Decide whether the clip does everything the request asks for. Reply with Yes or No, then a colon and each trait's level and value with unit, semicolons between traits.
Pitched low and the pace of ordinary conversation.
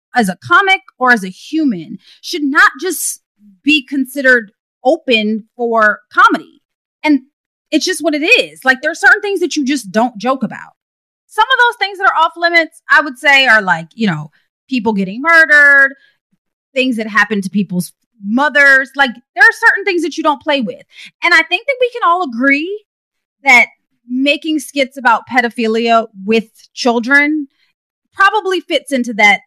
No: very high, 280 Hz; average, 175 wpm